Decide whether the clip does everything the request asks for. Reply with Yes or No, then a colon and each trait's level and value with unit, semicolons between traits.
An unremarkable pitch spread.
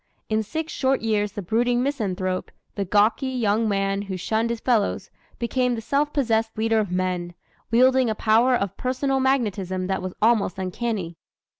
Yes: average, 4.0 semitones